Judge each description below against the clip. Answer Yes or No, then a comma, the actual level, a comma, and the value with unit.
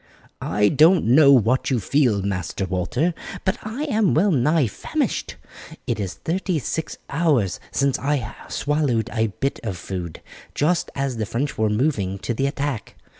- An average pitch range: No, wide, 6.4 semitones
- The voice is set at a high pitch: No, low, 135 Hz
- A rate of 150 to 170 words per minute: Yes, average, 160 wpm